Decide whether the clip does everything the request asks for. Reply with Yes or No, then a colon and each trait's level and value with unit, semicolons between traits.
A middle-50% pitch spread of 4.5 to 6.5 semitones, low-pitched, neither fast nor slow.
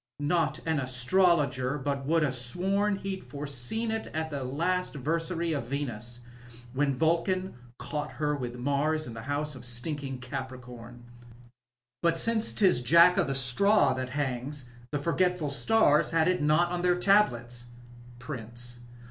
No: average, 5.0 semitones; medium, 145 Hz; average, 150 wpm